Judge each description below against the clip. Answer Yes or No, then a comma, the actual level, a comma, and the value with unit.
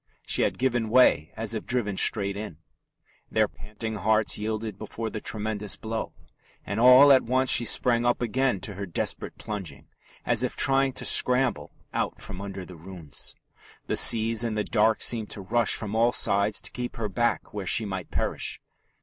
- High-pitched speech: No, low, 110 Hz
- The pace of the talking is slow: No, average, 185 wpm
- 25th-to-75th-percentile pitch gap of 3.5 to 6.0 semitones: No, average, 2.8 semitones